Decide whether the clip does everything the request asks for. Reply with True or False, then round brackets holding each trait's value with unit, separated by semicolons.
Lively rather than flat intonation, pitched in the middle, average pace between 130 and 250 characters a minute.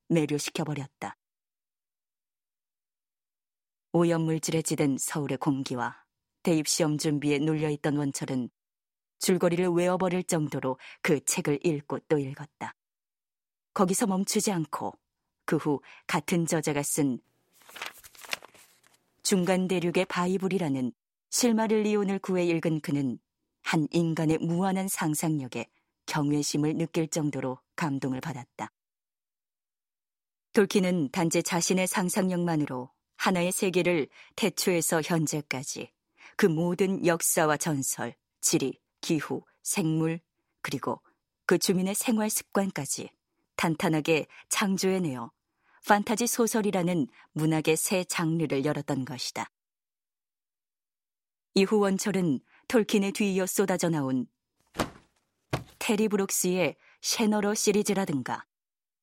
False (4.2 semitones; 170 Hz; 240 characters per minute)